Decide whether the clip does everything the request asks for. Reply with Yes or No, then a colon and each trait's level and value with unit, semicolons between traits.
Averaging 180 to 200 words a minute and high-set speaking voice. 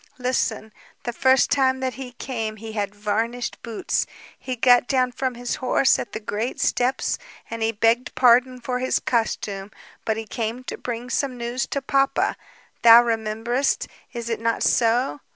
No: average, 170 wpm; high, 240 Hz